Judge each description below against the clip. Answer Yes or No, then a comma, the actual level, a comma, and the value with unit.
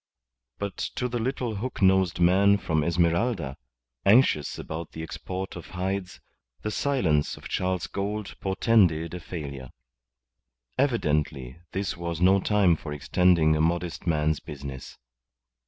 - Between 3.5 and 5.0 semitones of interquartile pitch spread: Yes, average, 4.1 semitones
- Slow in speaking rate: Yes, slow, 130 wpm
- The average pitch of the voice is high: No, very low, 90 Hz